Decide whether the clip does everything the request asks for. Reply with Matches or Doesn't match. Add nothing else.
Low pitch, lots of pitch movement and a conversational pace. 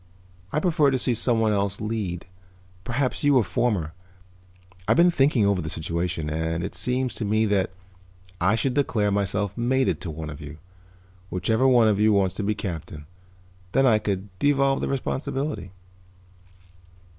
Matches